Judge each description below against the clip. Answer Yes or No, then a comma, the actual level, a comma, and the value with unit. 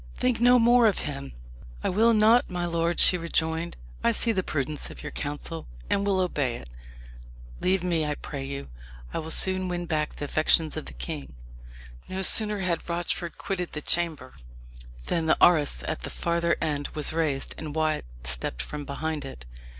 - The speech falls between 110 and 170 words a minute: No, average, 180 wpm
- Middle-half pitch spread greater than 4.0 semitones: No, average, 3.7 semitones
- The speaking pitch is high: No, medium, 165 Hz